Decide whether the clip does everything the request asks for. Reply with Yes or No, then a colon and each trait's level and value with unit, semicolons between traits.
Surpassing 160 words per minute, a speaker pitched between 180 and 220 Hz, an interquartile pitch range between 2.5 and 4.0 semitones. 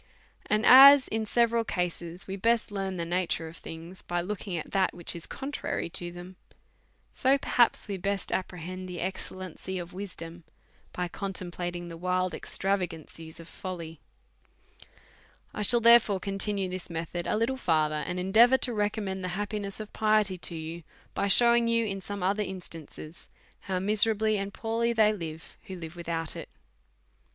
Yes: average, 170 wpm; high, 190 Hz; average, 3.5 semitones